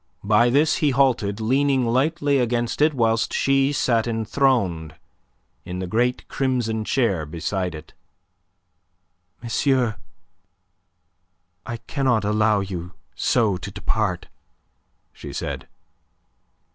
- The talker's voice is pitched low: Yes, low, 115 Hz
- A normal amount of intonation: Yes, average, 4.7 semitones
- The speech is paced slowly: Yes, slow, 105 wpm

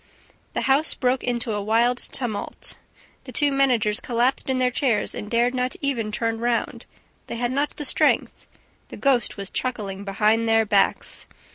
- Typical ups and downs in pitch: Yes, average, 3.0 semitones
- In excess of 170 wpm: No, average, 165 wpm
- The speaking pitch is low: No, high, 240 Hz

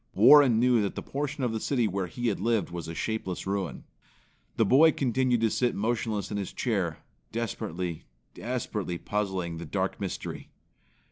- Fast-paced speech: No, average, 165 wpm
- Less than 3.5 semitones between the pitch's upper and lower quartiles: No, average, 4.4 semitones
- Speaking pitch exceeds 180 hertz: No, low, 110 Hz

